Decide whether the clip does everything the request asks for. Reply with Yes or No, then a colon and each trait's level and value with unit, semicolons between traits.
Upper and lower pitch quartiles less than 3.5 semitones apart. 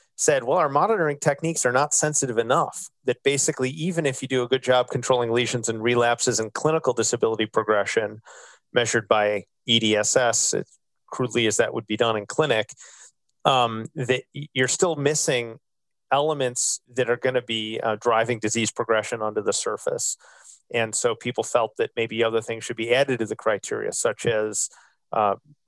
No: average, 4.5 semitones